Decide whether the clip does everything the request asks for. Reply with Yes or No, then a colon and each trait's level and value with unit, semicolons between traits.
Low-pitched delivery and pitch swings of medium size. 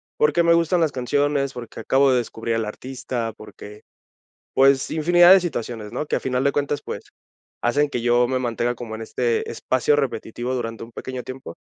Yes: low, 130 Hz; average, 3.5 semitones